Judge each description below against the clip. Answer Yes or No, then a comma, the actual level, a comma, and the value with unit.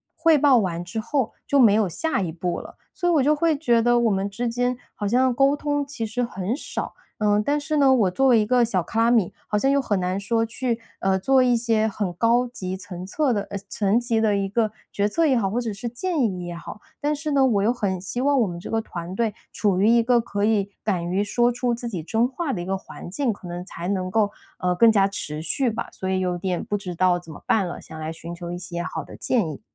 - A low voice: No, high, 220 Hz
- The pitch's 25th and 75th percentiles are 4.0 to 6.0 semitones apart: Yes, average, 4.8 semitones